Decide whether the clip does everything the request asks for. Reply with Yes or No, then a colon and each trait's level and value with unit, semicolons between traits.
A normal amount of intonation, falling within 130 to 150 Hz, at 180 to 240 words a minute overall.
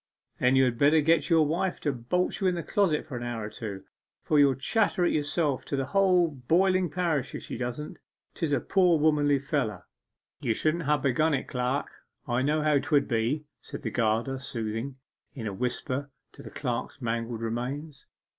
Yes: average, 4.4 semitones; medium, 140 Hz; average, 195 wpm